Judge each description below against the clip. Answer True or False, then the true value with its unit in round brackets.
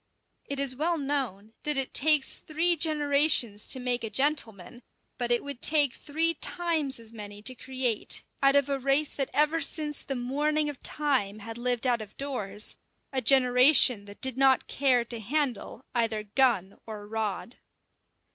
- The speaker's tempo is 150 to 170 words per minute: True (165 wpm)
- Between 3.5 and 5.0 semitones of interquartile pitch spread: True (4.2 semitones)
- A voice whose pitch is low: False (260 Hz)